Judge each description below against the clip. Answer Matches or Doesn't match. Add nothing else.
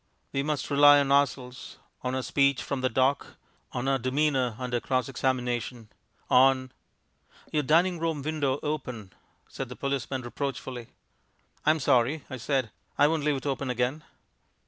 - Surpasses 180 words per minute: Doesn't match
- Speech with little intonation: Matches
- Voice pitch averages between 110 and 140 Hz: Matches